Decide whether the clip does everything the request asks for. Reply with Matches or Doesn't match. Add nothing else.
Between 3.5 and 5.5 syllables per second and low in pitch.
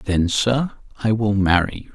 Matches